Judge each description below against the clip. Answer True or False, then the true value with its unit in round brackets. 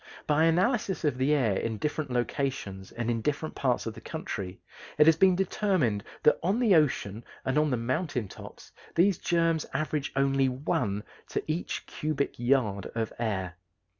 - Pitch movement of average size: False (5.8 semitones)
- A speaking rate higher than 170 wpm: False (165 wpm)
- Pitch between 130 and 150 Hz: True (140 Hz)